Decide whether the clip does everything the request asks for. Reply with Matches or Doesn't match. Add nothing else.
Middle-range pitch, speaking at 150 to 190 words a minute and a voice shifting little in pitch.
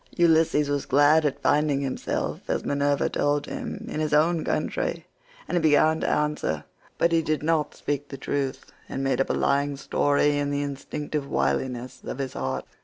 Matches